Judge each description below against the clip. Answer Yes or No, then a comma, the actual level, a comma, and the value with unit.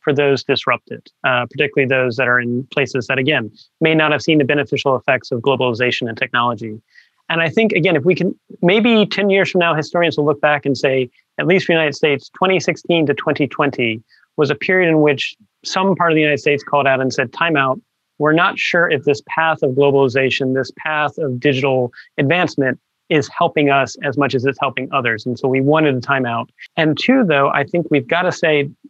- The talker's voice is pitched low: No, medium, 145 Hz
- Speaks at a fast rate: Yes, fast, 220 wpm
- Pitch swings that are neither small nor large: Yes, average, 3.4 semitones